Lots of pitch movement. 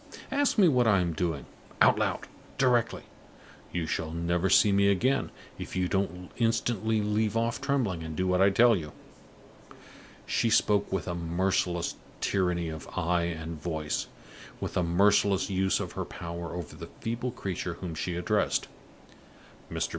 No: average, 4.0 semitones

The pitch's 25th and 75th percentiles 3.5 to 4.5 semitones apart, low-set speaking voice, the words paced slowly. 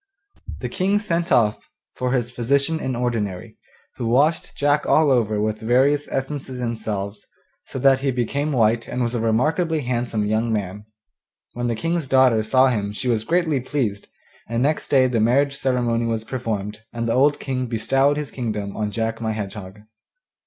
No: average, 3.9 semitones; low, 120 Hz; average, 175 wpm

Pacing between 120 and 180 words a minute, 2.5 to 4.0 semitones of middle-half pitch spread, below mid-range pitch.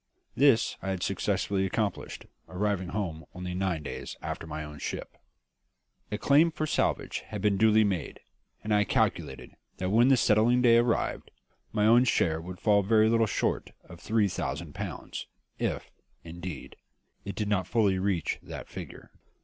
Yes: average, 160 wpm; average, 3.7 semitones; low, 100 Hz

